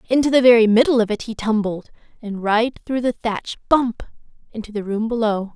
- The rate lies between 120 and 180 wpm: Yes, average, 175 wpm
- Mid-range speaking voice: No, high, 225 Hz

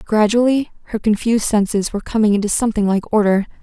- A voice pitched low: No, high, 215 Hz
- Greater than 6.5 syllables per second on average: Yes, 6.7 syllables/s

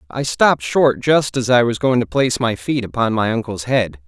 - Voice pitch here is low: Yes, low, 120 Hz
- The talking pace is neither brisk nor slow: No, fast, 235 wpm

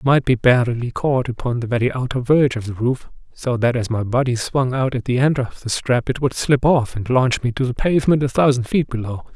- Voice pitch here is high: No, low, 125 Hz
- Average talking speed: No, fast, 255 wpm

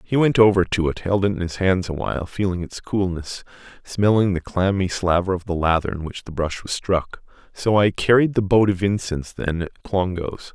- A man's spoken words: Yes, male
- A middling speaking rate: No, fast, 210 wpm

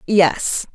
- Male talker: No, female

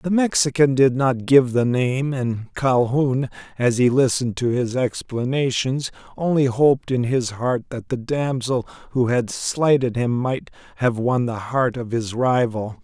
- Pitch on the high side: No, low, 125 Hz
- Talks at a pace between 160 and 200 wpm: Yes, average, 165 wpm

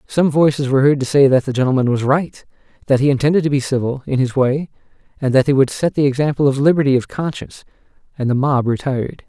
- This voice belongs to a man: Yes, male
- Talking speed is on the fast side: Yes, fast, 220 wpm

